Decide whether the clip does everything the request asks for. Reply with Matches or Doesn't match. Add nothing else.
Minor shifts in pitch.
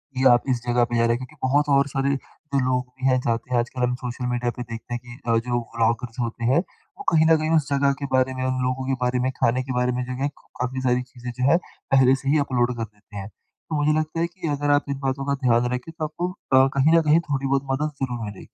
Matches